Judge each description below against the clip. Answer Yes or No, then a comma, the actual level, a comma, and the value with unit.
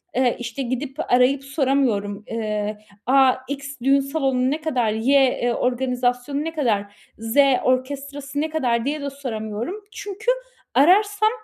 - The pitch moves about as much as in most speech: Yes, average, 3.0 semitones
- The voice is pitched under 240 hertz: No, very high, 265 Hz